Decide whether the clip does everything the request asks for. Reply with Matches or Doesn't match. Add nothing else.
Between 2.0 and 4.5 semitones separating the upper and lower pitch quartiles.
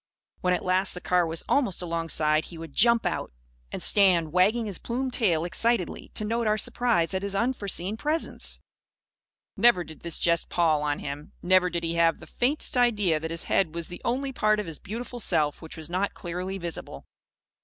Doesn't match